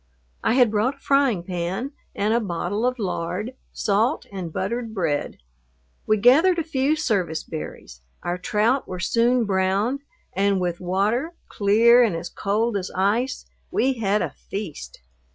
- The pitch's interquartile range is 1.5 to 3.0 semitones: No, average, 4.8 semitones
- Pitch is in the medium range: No, high, 210 Hz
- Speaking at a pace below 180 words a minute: Yes, average, 150 wpm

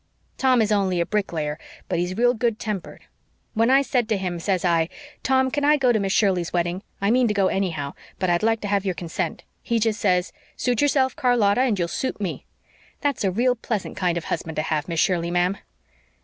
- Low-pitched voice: No, high, 200 Hz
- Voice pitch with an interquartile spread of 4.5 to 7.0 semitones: Yes, average, 5.3 semitones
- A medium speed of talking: No, fast, 220 wpm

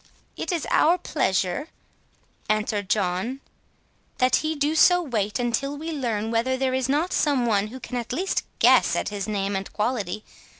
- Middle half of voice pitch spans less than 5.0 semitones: No, wide, 5.5 semitones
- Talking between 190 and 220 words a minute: No, average, 170 wpm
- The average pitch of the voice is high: Yes, high, 245 Hz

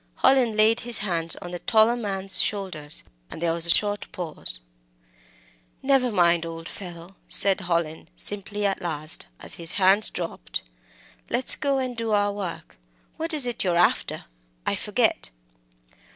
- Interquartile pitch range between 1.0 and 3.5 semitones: No, average, 4.6 semitones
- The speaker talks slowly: No, average, 150 wpm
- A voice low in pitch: No, high, 195 Hz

